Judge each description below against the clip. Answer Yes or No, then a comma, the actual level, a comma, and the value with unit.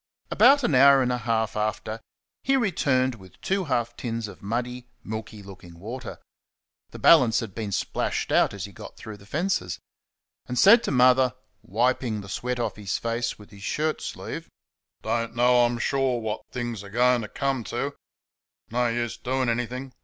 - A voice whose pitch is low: Yes, low, 120 Hz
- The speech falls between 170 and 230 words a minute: Yes, average, 175 wpm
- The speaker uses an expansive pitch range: No, average, 2.9 semitones